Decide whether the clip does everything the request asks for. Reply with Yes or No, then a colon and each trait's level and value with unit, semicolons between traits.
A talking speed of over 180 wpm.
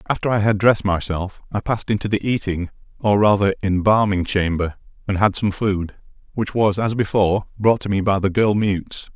Yes: average, 190 wpm